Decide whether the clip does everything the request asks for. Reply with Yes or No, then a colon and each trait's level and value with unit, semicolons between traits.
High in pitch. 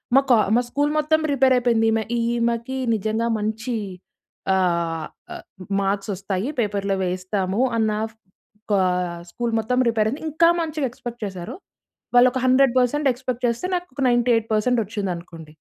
Yes: high, 230 Hz